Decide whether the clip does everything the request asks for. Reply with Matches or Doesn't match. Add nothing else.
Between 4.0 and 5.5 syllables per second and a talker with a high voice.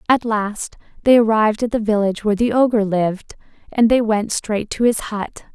Matches